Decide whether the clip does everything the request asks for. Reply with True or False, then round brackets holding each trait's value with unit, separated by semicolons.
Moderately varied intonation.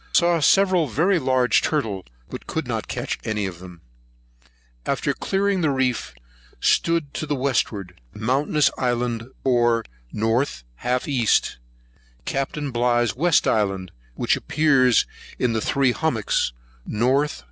True (4.8 semitones)